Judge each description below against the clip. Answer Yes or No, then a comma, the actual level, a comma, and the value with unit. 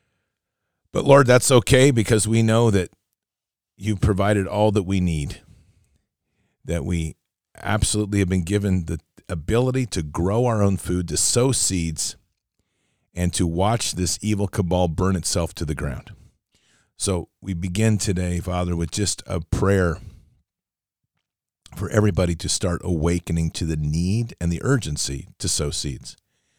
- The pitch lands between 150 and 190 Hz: No, very low, 95 Hz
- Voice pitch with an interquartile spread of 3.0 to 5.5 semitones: Yes, average, 3.5 semitones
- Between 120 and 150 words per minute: Yes, average, 145 wpm